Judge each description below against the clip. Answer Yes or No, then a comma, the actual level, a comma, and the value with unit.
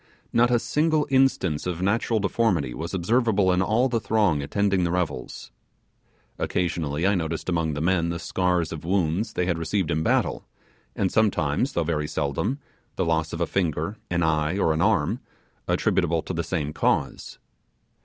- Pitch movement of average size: Yes, average, 4.1 semitones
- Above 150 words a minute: Yes, average, 170 wpm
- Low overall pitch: Yes, very low, 90 Hz